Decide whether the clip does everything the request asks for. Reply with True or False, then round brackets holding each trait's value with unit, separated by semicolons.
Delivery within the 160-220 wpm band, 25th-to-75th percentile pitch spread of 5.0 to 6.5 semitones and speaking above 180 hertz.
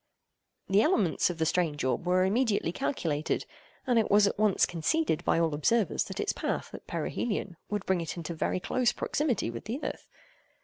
True (185 wpm; 5.4 semitones; 190 Hz)